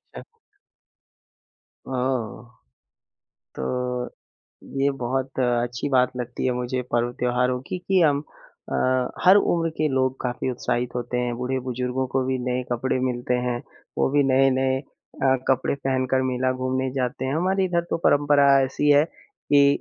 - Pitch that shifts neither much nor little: No, narrow, 1.5 semitones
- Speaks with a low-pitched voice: Yes, low, 130 Hz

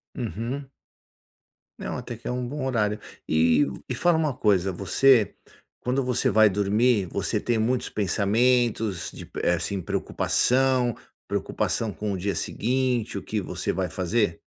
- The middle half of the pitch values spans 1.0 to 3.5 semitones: No, average, 4.2 semitones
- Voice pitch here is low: Yes, low, 110 Hz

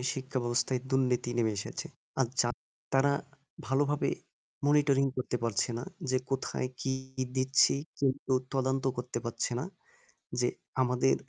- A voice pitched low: Yes, low, 130 Hz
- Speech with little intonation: Yes, narrow, 1.6 semitones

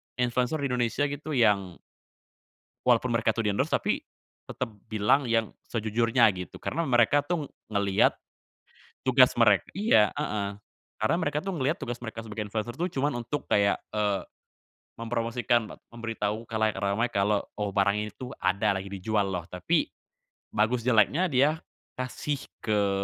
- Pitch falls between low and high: No, low, 115 Hz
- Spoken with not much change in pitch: No, average, 3.7 semitones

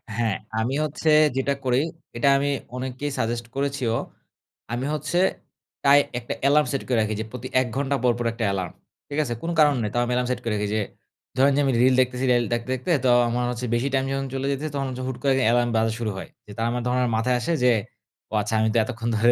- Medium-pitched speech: No, low, 125 Hz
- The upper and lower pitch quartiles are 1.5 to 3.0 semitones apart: Yes, narrow, 2.6 semitones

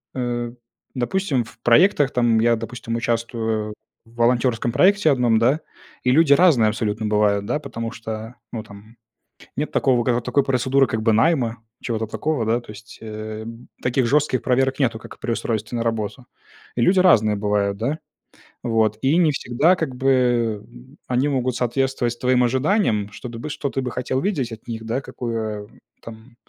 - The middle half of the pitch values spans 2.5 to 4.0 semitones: Yes, average, 3.0 semitones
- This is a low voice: Yes, low, 120 Hz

